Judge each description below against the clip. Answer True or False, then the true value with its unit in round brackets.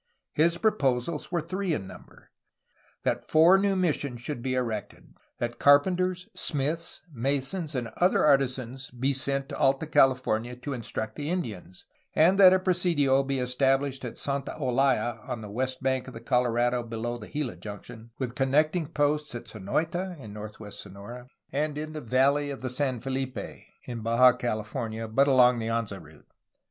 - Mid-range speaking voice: False (130 Hz)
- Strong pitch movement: False (3.9 semitones)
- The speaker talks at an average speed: True (165 wpm)